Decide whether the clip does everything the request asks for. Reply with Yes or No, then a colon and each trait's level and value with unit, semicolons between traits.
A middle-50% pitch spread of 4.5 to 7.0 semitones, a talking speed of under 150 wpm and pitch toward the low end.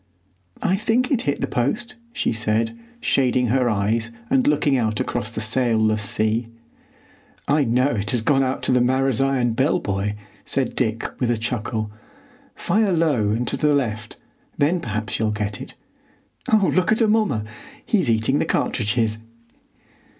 No: average, 4.9 semitones; average, 155 wpm; low, 120 Hz